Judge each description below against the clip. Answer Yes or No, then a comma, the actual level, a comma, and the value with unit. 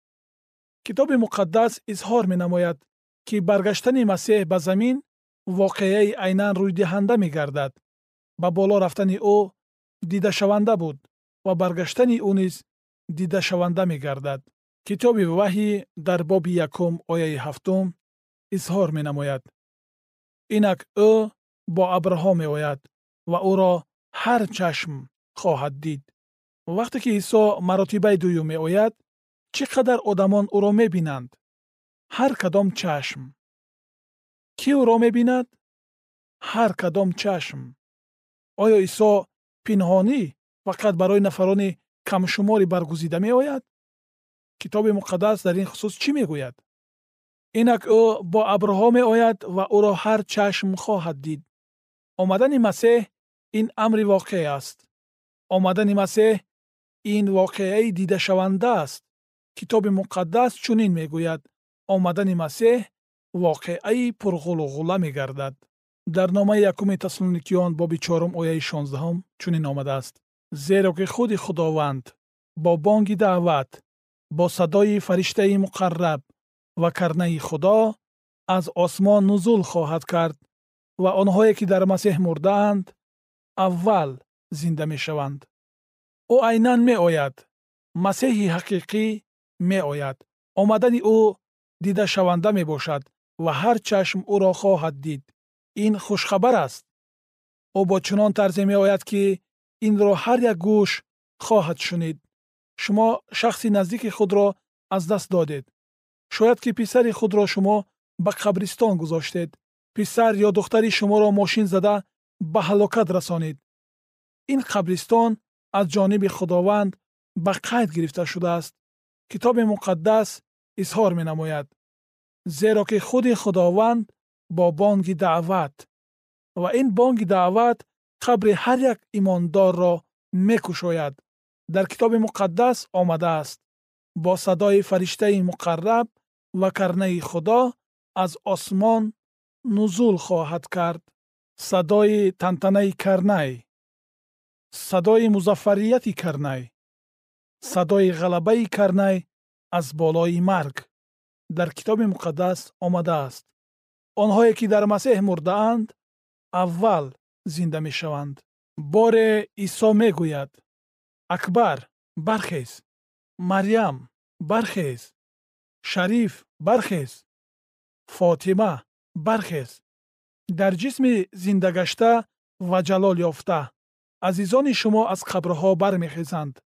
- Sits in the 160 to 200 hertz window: Yes, high, 190 Hz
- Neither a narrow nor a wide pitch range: Yes, average, 3.9 semitones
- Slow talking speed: Yes, slow, 100 wpm